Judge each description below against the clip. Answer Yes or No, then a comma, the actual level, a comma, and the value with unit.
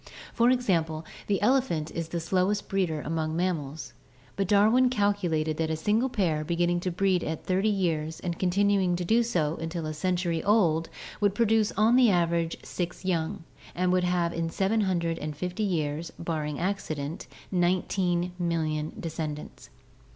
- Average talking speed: Yes, average, 150 wpm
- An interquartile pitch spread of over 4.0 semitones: No, average, 3.5 semitones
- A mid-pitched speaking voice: Yes, medium, 175 Hz